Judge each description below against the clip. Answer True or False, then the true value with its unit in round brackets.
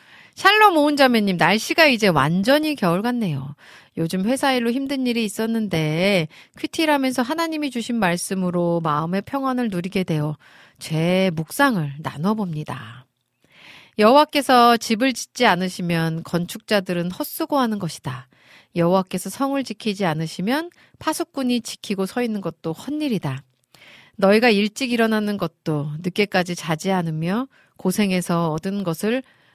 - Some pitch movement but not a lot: False (6.8 semitones)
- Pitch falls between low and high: False (195 Hz)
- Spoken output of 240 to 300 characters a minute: False (310 characters per minute)